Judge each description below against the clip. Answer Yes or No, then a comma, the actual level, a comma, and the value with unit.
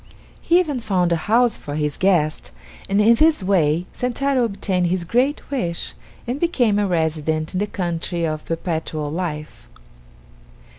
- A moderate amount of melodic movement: No, wide, 6.5 semitones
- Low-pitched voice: No, medium, 185 Hz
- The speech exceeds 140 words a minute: Yes, average, 150 wpm